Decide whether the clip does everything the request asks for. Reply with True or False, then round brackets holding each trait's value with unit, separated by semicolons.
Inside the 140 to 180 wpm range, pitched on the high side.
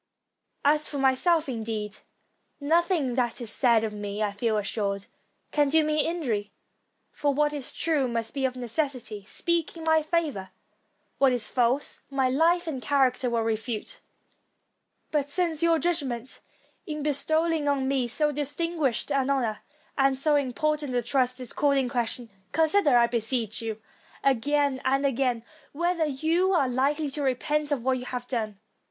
True (160 wpm; 270 Hz)